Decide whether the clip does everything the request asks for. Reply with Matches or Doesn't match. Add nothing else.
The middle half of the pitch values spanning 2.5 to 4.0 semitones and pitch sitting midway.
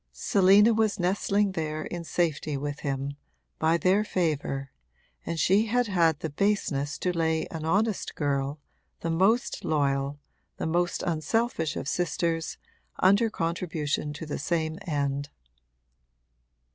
Doesn't match